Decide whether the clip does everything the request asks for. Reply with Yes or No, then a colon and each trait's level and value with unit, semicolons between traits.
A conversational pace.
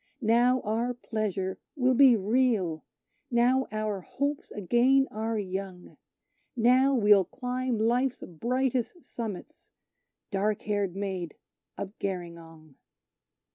No: slow, 100 wpm